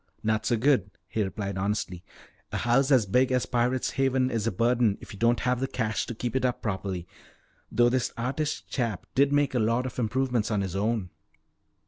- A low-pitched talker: Yes, low, 120 Hz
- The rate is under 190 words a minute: No, average, 200 wpm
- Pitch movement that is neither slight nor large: Yes, average, 3.5 semitones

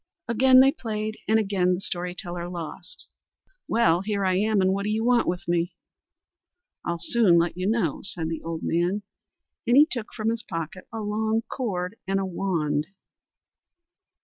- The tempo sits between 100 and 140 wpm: No, average, 175 wpm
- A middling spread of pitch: Yes, average, 3.9 semitones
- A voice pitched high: Yes, high, 195 Hz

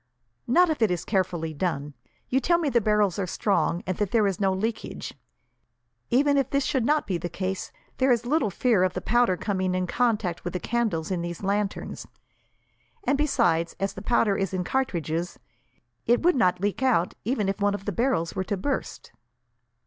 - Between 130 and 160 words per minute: No, average, 195 wpm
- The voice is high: Yes, high, 200 Hz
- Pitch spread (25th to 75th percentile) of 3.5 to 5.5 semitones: Yes, average, 5.0 semitones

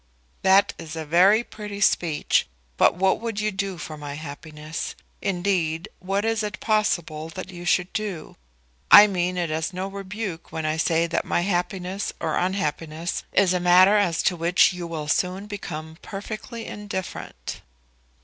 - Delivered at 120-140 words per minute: No, average, 160 wpm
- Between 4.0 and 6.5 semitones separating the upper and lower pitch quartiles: No, average, 3.6 semitones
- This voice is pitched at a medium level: Yes, medium, 180 Hz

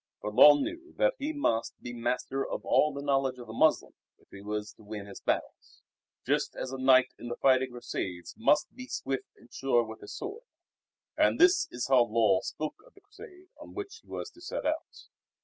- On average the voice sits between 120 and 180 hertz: Yes, low, 135 Hz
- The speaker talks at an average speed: No, fast, 210 wpm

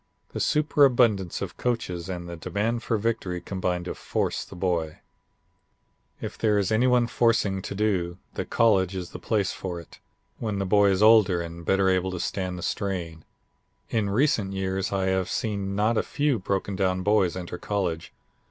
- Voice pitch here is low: Yes, very low, 95 Hz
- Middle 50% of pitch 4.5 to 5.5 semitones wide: No, average, 3.0 semitones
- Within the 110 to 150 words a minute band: No, average, 170 wpm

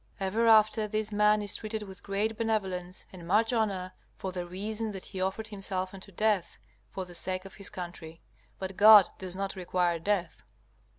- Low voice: No, high, 195 Hz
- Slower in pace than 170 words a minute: No, average, 180 wpm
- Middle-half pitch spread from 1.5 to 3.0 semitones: Yes, narrow, 2.5 semitones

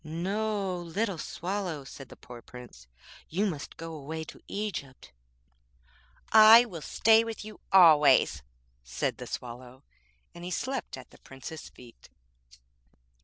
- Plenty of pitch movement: Yes, wide, 7.2 semitones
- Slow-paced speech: Yes, slow, 130 wpm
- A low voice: No, medium, 165 Hz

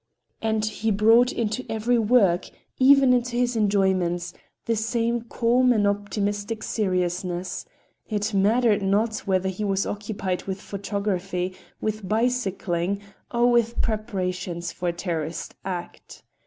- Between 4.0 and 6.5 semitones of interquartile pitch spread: No, average, 3.5 semitones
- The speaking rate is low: Yes, slow, 120 wpm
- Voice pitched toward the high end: Yes, high, 205 Hz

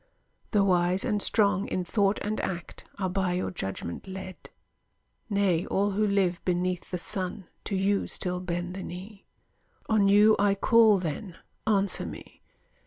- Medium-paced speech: Yes, average, 155 wpm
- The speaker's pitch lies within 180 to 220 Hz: Yes, high, 190 Hz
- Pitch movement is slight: Yes, narrow, 2.1 semitones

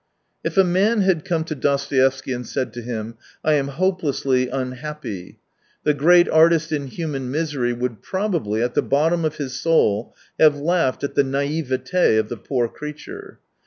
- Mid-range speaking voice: Yes, medium, 145 Hz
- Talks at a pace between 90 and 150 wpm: No, average, 170 wpm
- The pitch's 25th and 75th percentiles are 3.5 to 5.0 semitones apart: Yes, average, 4.3 semitones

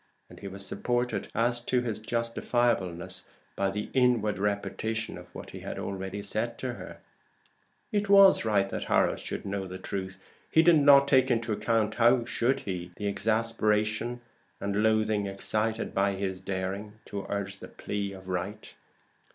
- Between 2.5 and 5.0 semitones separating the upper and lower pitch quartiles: Yes, average, 3.2 semitones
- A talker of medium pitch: No, low, 105 Hz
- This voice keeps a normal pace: Yes, average, 160 wpm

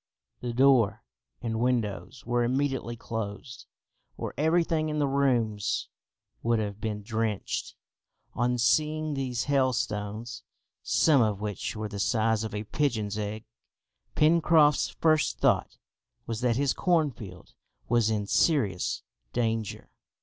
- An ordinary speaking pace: No, slow, 120 wpm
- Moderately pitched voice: No, low, 120 Hz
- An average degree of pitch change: Yes, average, 4.4 semitones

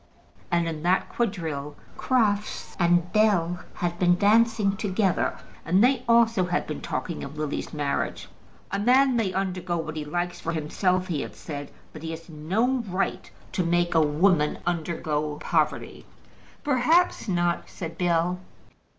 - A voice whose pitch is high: No, medium, 175 Hz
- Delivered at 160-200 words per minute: No, average, 150 wpm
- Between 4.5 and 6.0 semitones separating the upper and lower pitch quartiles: No, average, 3.9 semitones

